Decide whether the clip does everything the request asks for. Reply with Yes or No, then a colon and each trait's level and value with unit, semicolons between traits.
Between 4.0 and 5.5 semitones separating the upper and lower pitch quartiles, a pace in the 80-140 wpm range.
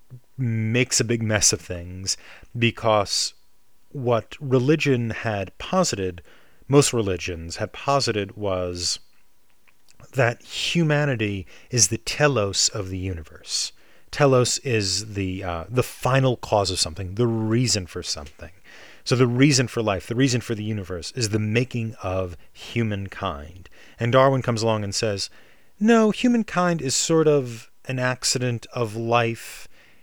Yes: average, 5.1 semitones; slow, 135 wpm